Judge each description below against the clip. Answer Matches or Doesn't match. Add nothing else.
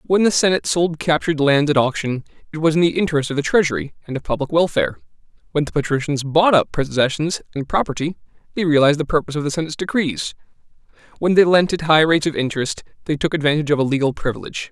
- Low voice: Doesn't match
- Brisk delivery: Matches